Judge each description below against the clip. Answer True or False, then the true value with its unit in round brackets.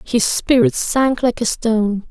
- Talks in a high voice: True (235 Hz)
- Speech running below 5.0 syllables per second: True (4.0 syllables/s)